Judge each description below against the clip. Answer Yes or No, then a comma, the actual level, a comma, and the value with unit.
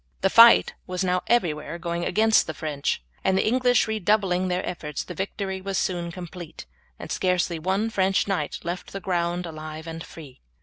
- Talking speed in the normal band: Yes, average, 175 wpm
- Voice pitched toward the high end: No, medium, 180 Hz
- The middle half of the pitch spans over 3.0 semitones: No, narrow, 2.6 semitones